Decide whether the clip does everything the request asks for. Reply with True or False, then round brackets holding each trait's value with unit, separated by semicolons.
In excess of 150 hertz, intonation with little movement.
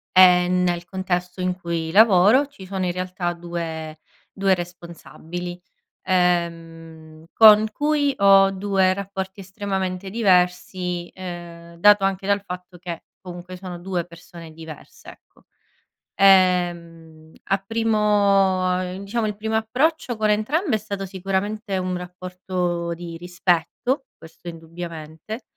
True (185 Hz; 2.3 semitones)